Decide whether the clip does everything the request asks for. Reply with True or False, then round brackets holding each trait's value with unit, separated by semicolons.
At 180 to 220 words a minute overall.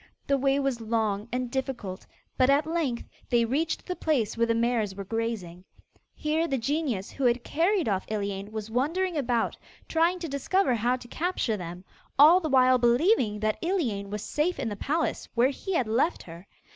True (185 wpm)